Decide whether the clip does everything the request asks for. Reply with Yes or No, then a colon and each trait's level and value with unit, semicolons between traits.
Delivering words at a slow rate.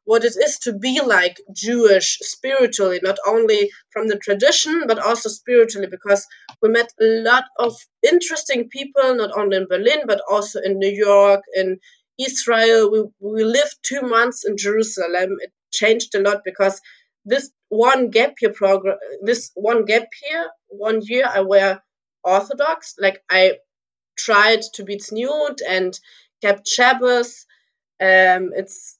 No: average, 150 wpm